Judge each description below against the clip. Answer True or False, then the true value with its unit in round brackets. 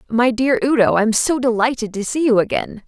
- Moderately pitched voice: False (245 Hz)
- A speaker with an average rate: False (210 wpm)